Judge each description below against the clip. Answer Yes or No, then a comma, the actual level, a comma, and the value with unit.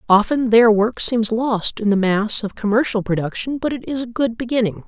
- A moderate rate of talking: No, fast, 210 wpm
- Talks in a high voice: Yes, high, 225 Hz